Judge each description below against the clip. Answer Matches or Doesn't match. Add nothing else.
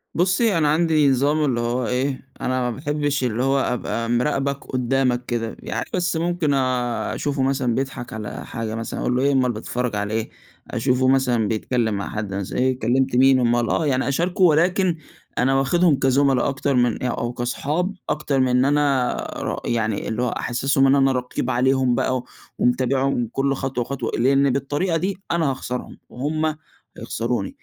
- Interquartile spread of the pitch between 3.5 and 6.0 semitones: Doesn't match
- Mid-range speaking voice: Doesn't match